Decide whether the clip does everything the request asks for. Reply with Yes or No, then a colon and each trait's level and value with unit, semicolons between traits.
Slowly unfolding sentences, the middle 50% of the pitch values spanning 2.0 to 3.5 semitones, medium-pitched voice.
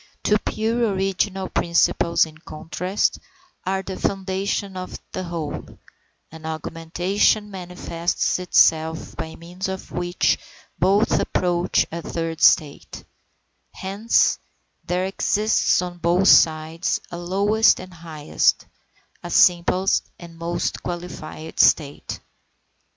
Yes: slow, 105 wpm; narrow, 2.6 semitones; medium, 180 Hz